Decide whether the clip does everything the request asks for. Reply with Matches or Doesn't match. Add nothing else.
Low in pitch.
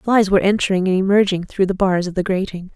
Doesn't match